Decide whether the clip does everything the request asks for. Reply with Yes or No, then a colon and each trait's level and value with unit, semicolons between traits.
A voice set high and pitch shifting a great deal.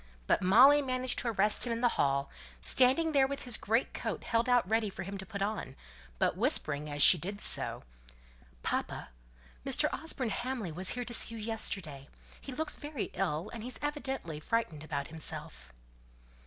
Yes: high, 220 Hz; wide, 7.0 semitones